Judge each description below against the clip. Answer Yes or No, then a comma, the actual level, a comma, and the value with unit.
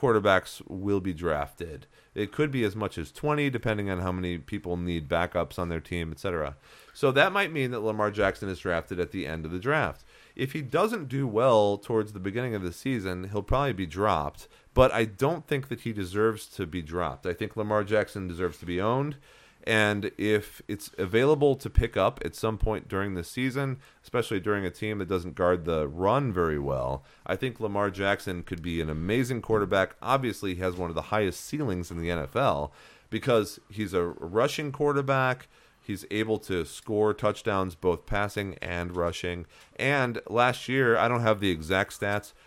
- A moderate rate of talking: Yes, average, 195 wpm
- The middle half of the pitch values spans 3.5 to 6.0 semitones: Yes, average, 4.1 semitones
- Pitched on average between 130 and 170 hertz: No, low, 100 Hz